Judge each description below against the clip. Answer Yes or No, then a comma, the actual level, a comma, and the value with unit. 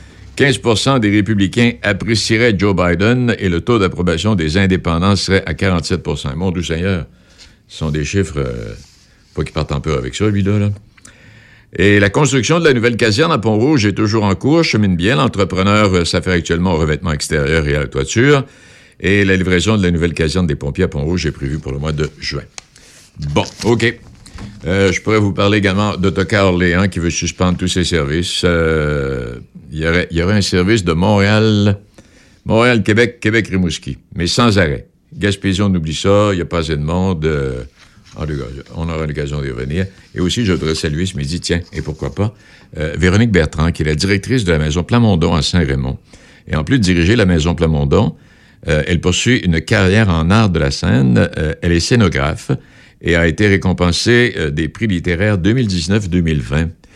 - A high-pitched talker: No, very low, 90 Hz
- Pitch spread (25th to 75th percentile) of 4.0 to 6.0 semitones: Yes, average, 4.6 semitones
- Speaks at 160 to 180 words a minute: No, average, 190 wpm